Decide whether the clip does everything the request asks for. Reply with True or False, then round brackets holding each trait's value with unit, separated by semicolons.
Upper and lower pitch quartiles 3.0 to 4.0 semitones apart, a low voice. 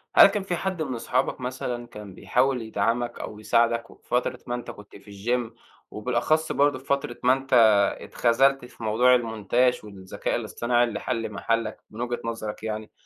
False (2.4 semitones; 120 Hz)